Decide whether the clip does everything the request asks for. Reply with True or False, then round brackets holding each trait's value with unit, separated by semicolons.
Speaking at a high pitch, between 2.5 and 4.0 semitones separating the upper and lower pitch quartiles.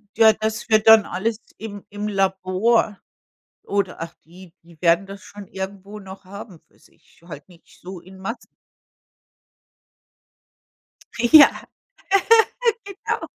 True (195 Hz; 2.8 semitones)